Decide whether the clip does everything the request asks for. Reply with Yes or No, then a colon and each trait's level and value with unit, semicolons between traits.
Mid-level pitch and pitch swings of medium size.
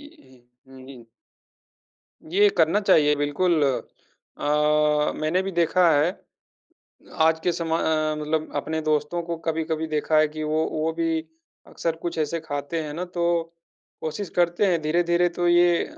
No: medium, 160 Hz; narrow, 2.1 semitones